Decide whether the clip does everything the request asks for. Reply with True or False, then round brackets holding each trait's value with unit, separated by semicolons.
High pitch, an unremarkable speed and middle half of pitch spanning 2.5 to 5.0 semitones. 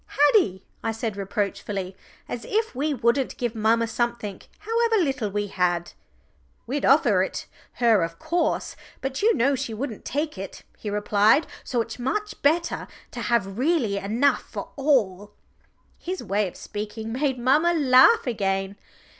False (235 Hz; 150 wpm; 5.6 semitones)